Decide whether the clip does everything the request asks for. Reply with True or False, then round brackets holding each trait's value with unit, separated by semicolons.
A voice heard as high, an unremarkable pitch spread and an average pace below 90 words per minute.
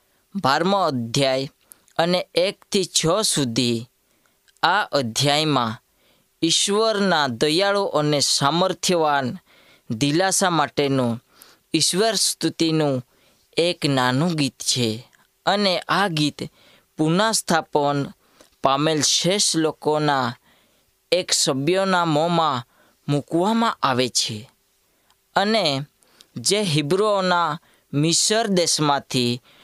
False (150 Hz; 4.8 semitones; 75 wpm)